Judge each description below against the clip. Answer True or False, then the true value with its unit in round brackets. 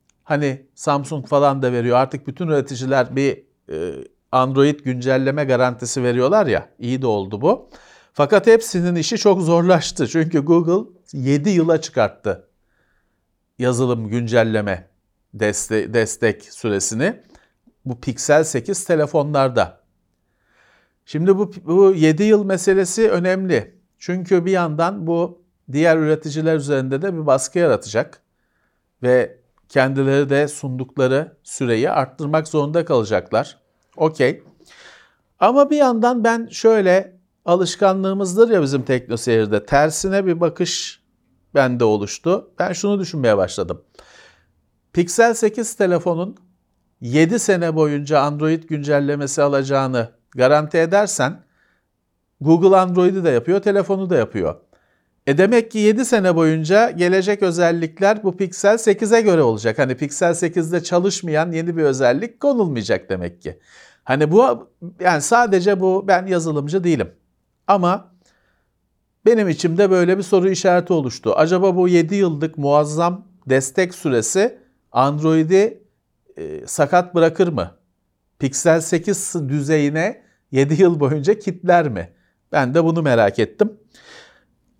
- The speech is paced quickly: False (115 wpm)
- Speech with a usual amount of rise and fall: False (5.9 semitones)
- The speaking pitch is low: False (165 Hz)